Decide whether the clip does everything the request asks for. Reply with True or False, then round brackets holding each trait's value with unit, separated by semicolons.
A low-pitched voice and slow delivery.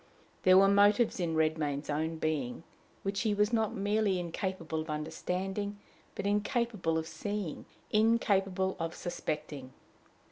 False (185 Hz; 130 wpm)